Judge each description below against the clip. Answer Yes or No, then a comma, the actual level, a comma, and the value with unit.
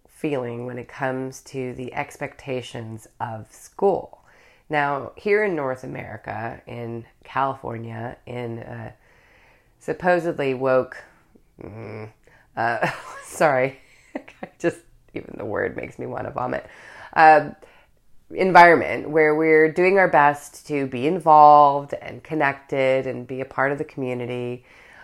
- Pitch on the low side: Yes, low, 130 Hz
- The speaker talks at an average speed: No, slow, 120 wpm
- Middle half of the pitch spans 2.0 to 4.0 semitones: Yes, average, 3.6 semitones